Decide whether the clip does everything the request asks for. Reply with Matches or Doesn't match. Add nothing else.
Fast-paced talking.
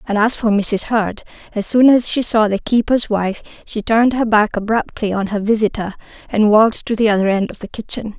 Matches